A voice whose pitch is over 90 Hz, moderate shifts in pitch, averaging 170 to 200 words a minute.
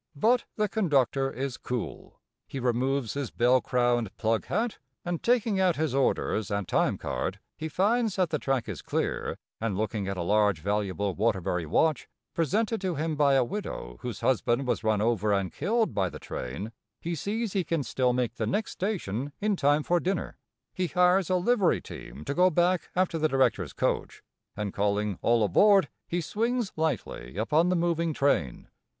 No: medium, 140 Hz; wide, 8.7 semitones; average, 180 wpm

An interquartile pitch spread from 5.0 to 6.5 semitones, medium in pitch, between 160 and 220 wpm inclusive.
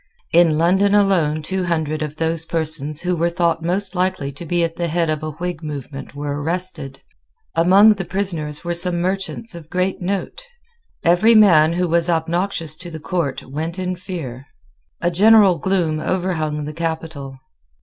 No: average, 2.9 semitones; medium, 170 Hz; average, 170 wpm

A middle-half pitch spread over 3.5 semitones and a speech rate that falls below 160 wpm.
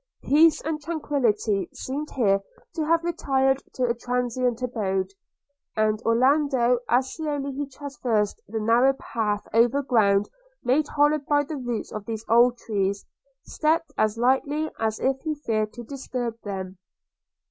Yes: average, 4.6 semitones; average, 145 wpm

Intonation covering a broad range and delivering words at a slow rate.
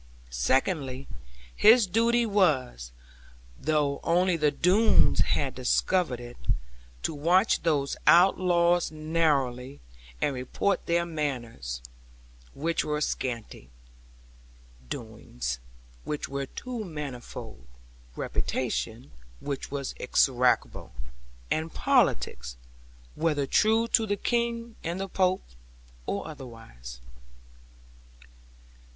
Yes: wide, 6.3 semitones; slow, 95 wpm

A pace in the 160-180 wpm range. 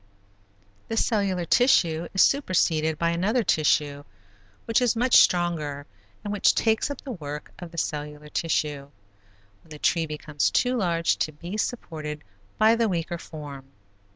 No: average, 150 wpm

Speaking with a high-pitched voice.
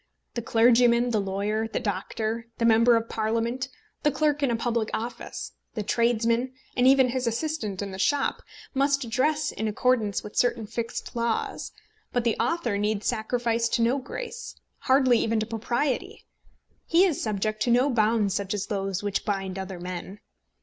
Yes: high, 230 Hz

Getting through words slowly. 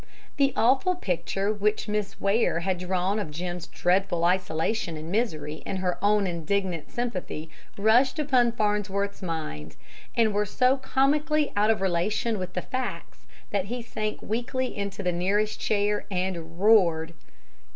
No: average, 145 wpm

